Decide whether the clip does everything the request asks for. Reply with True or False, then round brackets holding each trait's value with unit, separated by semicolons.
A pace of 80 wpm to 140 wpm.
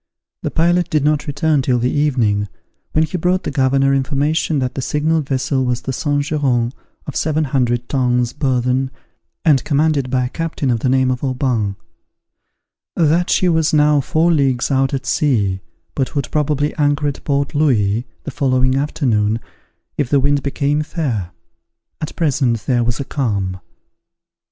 False (165 wpm)